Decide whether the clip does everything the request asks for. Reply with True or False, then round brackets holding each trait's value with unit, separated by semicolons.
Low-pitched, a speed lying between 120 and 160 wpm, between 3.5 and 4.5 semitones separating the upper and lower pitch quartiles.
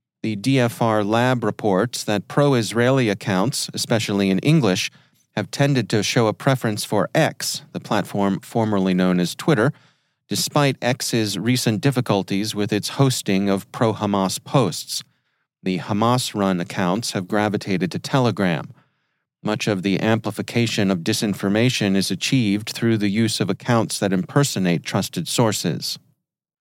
True (110 Hz; 140 wpm; 4.1 semitones)